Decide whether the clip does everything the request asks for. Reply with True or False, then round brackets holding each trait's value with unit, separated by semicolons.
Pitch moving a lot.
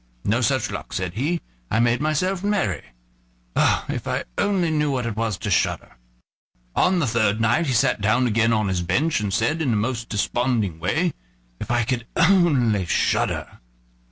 True (6.2 semitones)